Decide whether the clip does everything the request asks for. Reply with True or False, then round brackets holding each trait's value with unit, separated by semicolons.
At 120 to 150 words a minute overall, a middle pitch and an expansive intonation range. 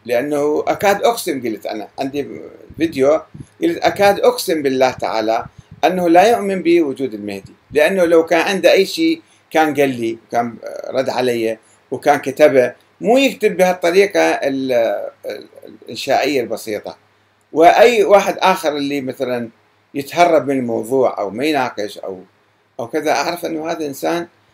True (130 wpm; 150 Hz; 7.6 semitones)